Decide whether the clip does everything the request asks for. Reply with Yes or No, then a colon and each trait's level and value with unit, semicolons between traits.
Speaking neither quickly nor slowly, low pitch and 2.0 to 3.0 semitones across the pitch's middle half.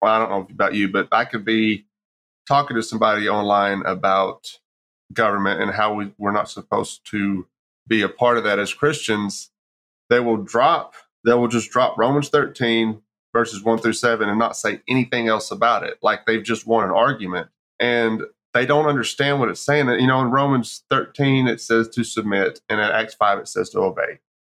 Yes: average, 195 wpm; low, 110 Hz; average, 2.7 semitones